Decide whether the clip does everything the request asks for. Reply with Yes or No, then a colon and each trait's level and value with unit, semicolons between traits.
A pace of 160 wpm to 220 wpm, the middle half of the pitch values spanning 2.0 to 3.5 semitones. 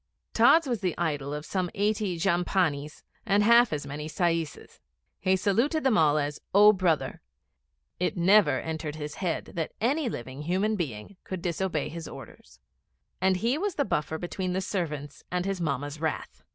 No: average, 165 wpm; average, 4.9 semitones